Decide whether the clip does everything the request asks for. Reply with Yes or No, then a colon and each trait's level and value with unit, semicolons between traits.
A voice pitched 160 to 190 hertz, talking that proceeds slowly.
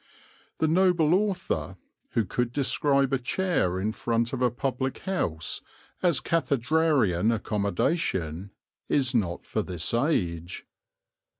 No: low, 125 Hz; slow, 115 wpm